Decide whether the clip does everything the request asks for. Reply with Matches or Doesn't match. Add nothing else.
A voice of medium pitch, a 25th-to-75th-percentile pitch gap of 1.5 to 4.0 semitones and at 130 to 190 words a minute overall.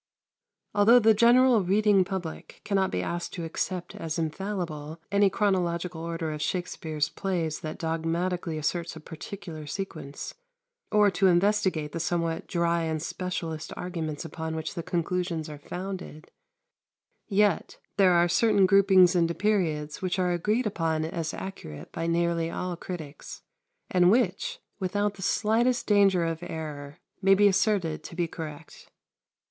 Matches